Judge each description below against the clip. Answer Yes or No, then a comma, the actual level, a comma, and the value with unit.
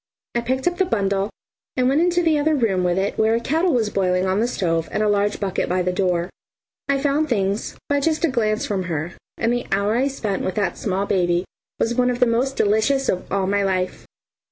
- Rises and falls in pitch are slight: No, wide, 5.6 semitones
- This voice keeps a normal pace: No, fast, 230 wpm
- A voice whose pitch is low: No, high, 215 Hz